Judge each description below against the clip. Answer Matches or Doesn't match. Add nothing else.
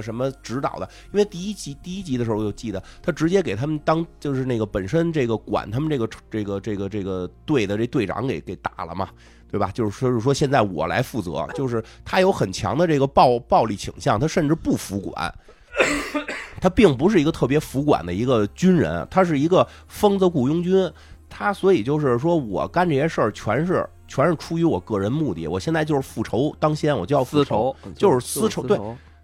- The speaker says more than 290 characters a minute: Matches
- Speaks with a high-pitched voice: Doesn't match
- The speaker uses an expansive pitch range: Matches